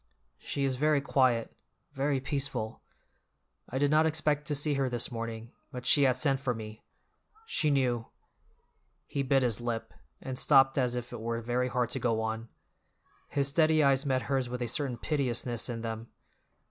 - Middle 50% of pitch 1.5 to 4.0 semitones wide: Yes, average, 3.0 semitones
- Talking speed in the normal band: Yes, average, 170 wpm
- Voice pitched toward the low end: Yes, low, 130 Hz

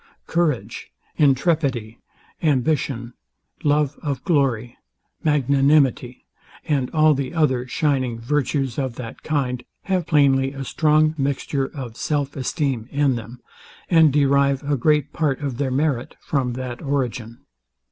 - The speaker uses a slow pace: Yes, slow, 125 wpm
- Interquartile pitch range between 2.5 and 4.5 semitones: Yes, average, 2.9 semitones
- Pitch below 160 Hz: Yes, medium, 140 Hz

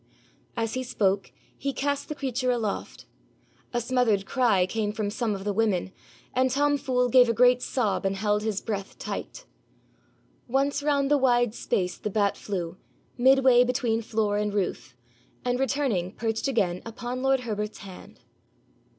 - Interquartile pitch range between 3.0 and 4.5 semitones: Yes, average, 3.9 semitones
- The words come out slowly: No, average, 160 wpm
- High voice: Yes, high, 230 Hz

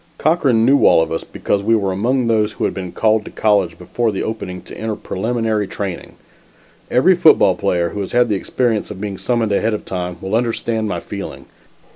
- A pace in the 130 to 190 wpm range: No, fast, 205 wpm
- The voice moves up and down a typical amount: Yes, average, 3.3 semitones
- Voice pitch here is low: Yes, low, 105 Hz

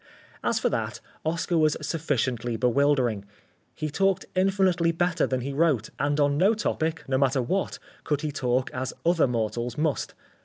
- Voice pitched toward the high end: No, medium, 145 Hz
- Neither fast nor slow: Yes, average, 160 wpm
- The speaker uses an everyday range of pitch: Yes, average, 4.7 semitones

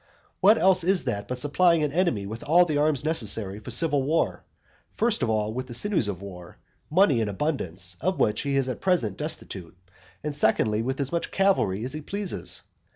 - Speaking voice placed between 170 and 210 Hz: No, low, 135 Hz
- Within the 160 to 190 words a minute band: No, average, 200 wpm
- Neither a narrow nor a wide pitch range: No, wide, 7.9 semitones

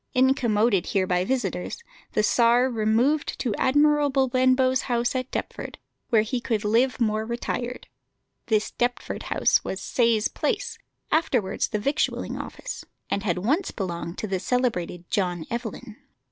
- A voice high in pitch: Yes, high, 235 Hz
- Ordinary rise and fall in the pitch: Yes, average, 3.7 semitones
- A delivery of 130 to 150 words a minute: Yes, average, 140 wpm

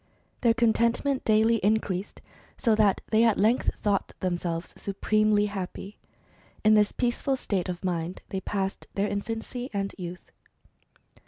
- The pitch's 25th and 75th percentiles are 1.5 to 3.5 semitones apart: Yes, average, 2.9 semitones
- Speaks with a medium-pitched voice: No, high, 210 Hz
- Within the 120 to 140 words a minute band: Yes, slow, 135 wpm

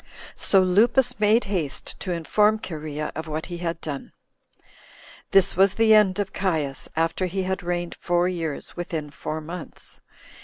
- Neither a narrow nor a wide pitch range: Yes, average, 3.5 semitones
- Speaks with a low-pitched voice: No, medium, 175 Hz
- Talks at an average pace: Yes, average, 160 wpm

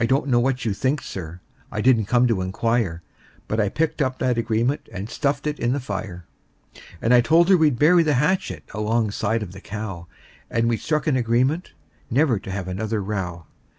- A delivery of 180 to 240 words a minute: Yes, average, 200 wpm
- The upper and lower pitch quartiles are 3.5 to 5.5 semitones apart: Yes, average, 4.9 semitones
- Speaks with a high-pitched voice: No, low, 115 Hz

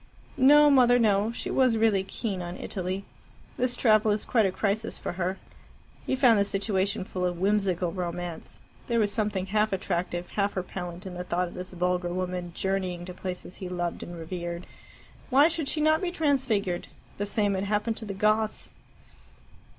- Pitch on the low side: No, high, 195 Hz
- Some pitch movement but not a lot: Yes, average, 3.6 semitones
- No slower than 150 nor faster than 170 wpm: No, average, 180 wpm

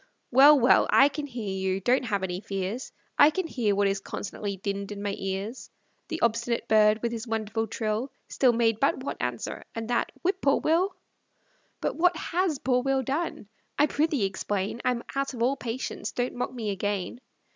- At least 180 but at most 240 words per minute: Yes, average, 190 wpm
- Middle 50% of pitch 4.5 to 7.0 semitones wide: Yes, average, 5.0 semitones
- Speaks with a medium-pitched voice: No, high, 235 Hz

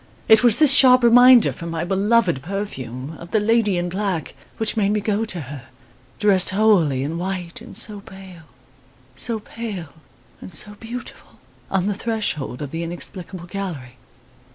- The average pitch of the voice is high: Yes, high, 195 Hz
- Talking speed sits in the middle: Yes, average, 165 wpm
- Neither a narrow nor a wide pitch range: Yes, average, 4.6 semitones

